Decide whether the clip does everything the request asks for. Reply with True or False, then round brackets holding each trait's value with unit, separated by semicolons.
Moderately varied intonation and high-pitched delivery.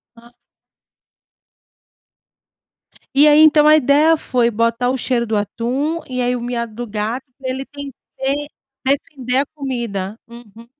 True (3.4 semitones; 250 Hz)